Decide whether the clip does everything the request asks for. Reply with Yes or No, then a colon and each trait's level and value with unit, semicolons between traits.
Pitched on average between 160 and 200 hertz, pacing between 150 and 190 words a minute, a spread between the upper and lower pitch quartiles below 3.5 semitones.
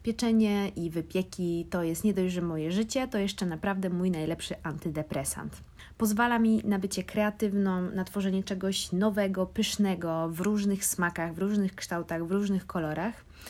Yes: high, 190 Hz; average, 155 wpm; average, 3.1 semitones